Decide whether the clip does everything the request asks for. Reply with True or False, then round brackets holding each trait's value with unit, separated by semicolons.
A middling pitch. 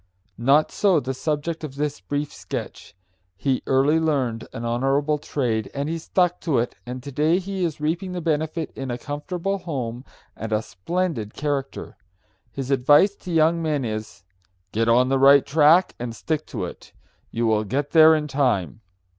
True (145 Hz)